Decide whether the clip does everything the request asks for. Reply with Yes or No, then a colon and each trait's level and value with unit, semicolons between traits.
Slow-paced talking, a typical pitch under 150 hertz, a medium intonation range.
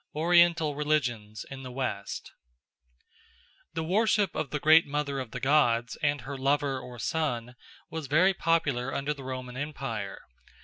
No: average, 145 wpm; medium, 140 Hz; average, 3.8 semitones